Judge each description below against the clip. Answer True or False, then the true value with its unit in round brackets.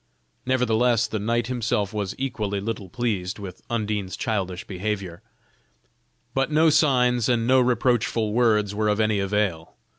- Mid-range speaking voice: False (110 Hz)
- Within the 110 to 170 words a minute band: True (140 wpm)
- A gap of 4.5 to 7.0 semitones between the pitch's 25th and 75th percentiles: False (3.3 semitones)